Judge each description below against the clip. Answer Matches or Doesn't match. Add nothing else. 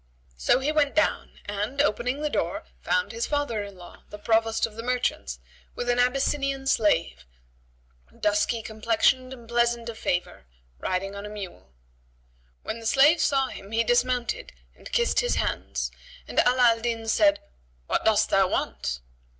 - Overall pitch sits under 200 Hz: Doesn't match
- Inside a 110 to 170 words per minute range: Matches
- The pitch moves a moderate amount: Matches